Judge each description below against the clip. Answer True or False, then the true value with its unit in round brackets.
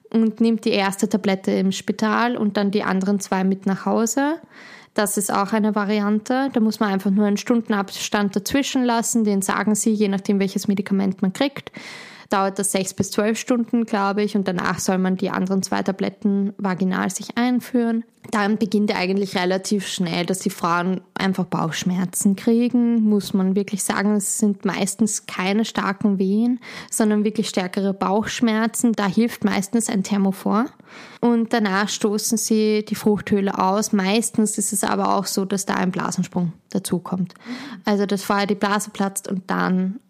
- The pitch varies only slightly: True (2.1 semitones)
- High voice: True (205 Hz)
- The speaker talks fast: False (170 wpm)